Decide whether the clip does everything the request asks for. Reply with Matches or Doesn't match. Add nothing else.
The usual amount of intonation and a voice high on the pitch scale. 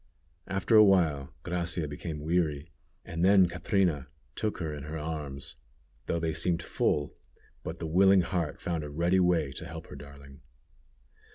Doesn't match